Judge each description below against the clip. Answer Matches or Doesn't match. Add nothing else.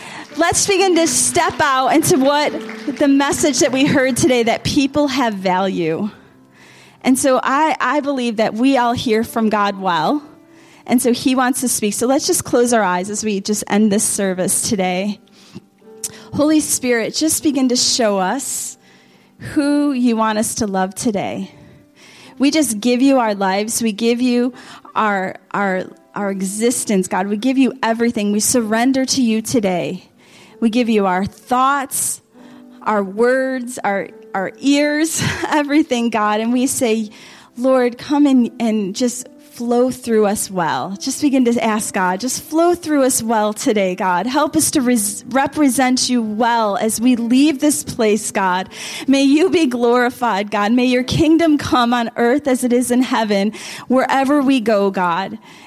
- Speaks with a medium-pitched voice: Doesn't match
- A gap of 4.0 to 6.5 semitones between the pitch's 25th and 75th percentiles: Matches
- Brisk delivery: Matches